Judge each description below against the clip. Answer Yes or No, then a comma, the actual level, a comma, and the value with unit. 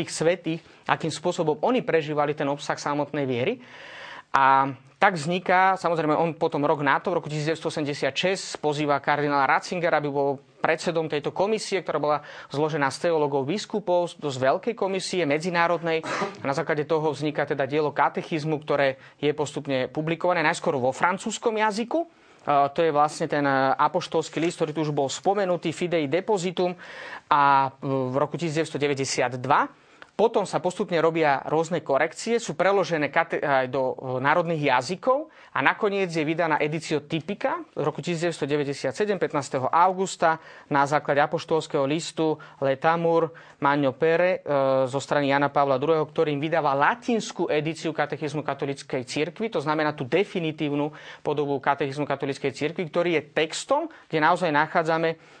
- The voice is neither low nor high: Yes, medium, 155 Hz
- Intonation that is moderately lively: Yes, average, 3.1 semitones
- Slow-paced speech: No, average, 140 wpm